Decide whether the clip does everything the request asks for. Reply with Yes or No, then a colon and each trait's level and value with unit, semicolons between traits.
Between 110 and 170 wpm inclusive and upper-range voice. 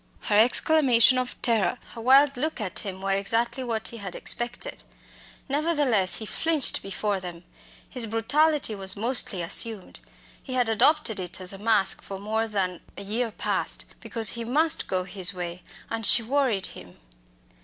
Yes: average, 165 wpm; high, 225 Hz